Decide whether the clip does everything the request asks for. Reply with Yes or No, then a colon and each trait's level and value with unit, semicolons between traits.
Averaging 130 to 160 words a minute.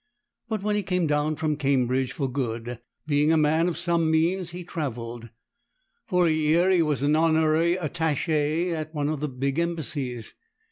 No: average, 175 wpm